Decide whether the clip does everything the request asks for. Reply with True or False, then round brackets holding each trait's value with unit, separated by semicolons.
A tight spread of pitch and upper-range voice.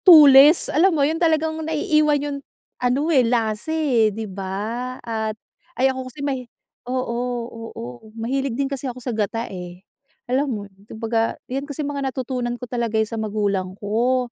False (4.3 semitones; 250 Hz)